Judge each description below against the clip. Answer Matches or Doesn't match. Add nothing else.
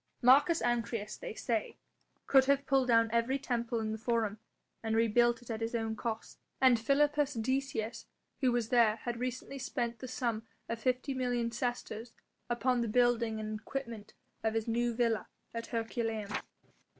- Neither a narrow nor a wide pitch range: Doesn't match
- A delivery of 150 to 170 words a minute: Matches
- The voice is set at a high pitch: Matches